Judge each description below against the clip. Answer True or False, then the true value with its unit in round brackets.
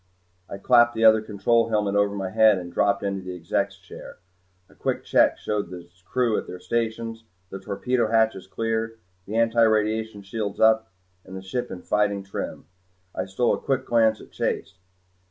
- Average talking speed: True (175 wpm)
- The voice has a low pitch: True (110 Hz)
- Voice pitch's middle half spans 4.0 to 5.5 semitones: False (2.5 semitones)